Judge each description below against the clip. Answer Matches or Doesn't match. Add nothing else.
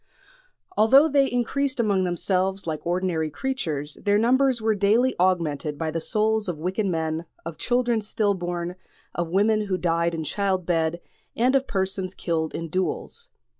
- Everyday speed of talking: Matches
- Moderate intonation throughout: Matches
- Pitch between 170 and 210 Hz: Matches